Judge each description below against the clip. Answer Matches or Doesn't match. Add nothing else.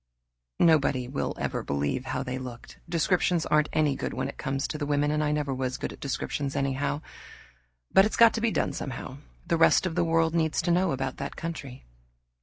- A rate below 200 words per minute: Doesn't match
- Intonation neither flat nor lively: Matches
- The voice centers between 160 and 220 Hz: Doesn't match